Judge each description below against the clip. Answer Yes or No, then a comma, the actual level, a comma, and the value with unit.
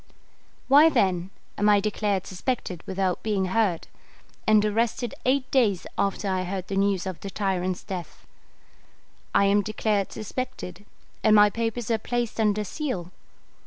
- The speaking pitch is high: Yes, high, 205 Hz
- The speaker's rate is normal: Yes, average, 145 wpm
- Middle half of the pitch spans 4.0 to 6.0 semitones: No, average, 2.9 semitones